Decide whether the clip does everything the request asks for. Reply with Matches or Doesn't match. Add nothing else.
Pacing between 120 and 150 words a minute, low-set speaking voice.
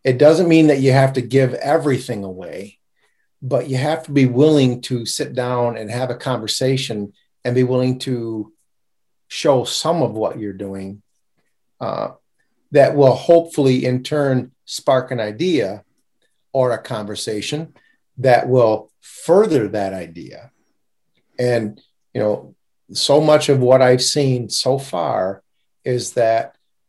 Matches